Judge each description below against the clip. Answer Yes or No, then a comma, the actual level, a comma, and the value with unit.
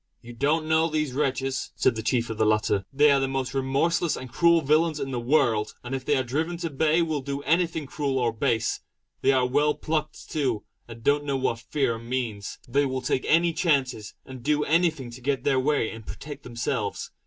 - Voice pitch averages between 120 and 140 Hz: Yes, low, 135 Hz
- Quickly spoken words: Yes, fast, 215 wpm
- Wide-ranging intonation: No, average, 3.7 semitones